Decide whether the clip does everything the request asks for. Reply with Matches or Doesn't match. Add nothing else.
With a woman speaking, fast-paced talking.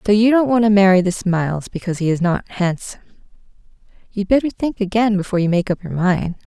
Matches